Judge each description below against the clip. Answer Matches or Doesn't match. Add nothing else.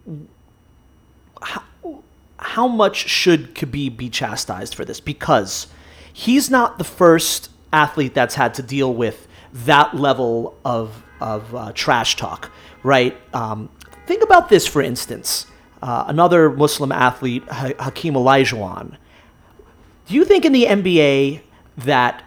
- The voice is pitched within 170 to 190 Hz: Doesn't match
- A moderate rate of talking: Doesn't match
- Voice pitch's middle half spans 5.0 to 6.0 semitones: Matches